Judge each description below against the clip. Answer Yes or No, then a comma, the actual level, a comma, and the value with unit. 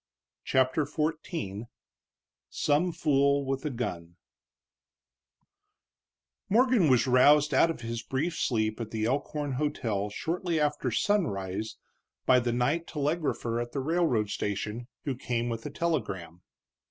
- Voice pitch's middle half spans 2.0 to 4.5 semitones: No, average, 5.0 semitones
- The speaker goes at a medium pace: No, slow, 125 wpm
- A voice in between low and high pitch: No, low, 130 Hz